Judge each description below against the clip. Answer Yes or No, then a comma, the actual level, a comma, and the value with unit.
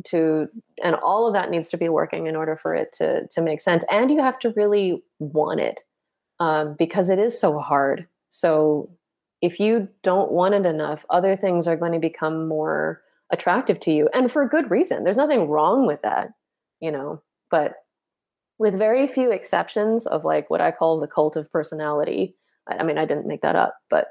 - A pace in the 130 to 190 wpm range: No, average, 200 wpm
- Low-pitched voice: No, medium, 175 Hz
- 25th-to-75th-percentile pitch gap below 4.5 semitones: No, average, 5.2 semitones